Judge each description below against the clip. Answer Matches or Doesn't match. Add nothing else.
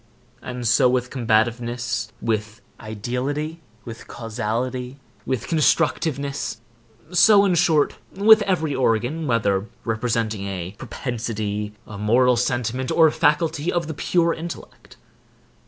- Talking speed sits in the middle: Doesn't match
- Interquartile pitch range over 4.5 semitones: Matches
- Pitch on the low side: Matches